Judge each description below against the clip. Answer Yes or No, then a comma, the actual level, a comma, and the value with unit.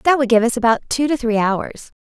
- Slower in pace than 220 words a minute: No, fast, 265 wpm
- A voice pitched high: Yes, high, 240 Hz